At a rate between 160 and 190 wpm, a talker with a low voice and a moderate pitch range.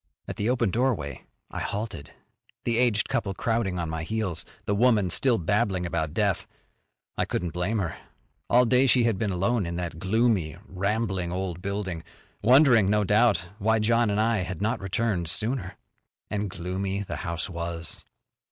Yes: average, 165 wpm; low, 100 Hz; average, 4.3 semitones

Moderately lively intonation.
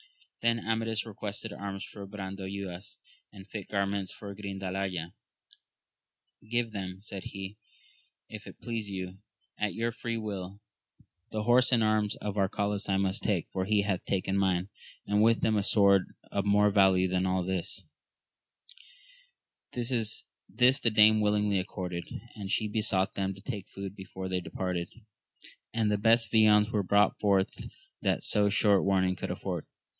No: narrow, 2.1 semitones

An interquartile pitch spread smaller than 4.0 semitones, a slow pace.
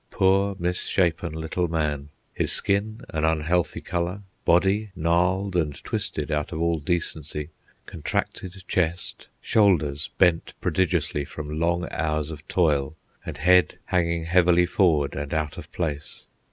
Yes: average, 2.9 semitones; slow, 130 wpm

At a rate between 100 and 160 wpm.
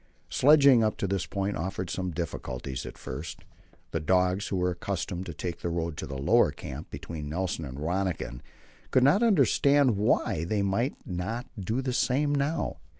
No: average, 175 wpm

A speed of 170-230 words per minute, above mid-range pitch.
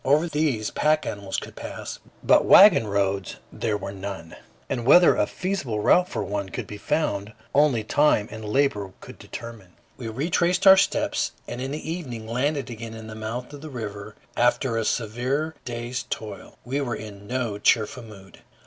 No: average, 175 wpm; low, 115 Hz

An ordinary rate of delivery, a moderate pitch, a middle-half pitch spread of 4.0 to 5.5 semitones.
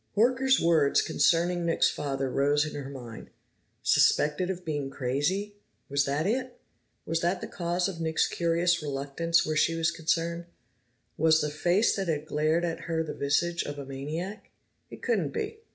No: average, 170 wpm; medium, 165 Hz; average, 3.2 semitones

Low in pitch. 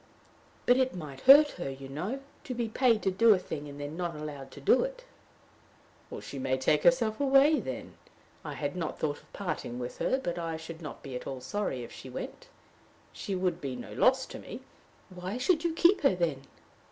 No: medium, 175 Hz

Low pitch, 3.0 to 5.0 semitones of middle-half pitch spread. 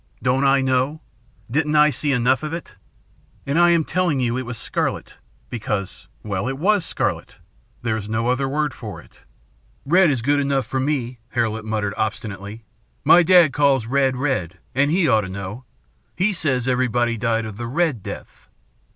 Yes: low, 130 Hz; average, 4.6 semitones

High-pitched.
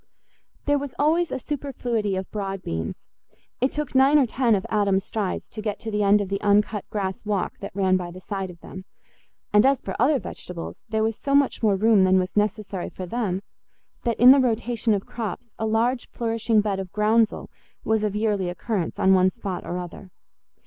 Yes: high, 210 Hz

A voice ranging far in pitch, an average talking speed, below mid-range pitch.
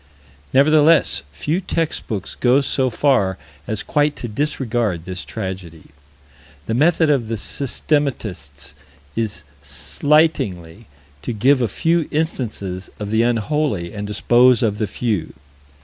No: wide, 6.6 semitones; slow, 125 wpm; low, 115 Hz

